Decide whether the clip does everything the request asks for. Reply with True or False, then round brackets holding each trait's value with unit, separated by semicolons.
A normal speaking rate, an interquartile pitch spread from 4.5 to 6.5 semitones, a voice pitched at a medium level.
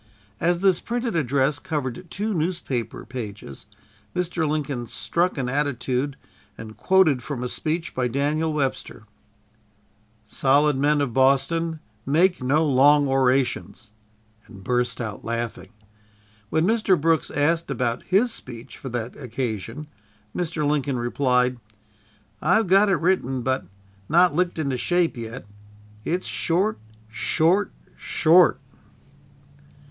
False (120 wpm; 5.1 semitones; 145 Hz)